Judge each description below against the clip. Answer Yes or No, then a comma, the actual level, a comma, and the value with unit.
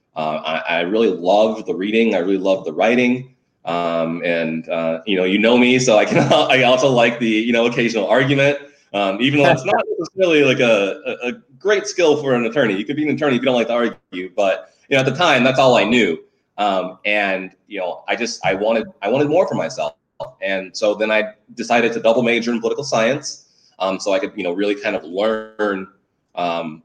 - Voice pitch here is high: No, low, 115 Hz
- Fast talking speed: Yes, fast, 230 wpm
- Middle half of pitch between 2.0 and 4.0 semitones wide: No, average, 4.8 semitones